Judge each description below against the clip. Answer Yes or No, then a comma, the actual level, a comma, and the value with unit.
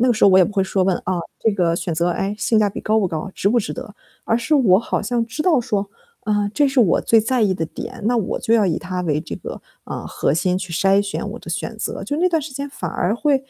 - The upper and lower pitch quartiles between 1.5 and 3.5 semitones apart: No, average, 4.5 semitones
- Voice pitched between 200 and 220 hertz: Yes, high, 205 Hz